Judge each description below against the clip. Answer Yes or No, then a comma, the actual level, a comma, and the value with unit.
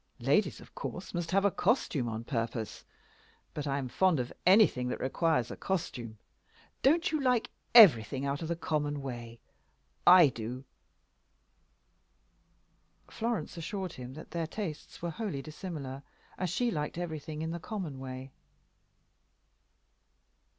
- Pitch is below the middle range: No, medium, 155 Hz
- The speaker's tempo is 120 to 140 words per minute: Yes, slow, 135 wpm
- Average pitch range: No, wide, 6.0 semitones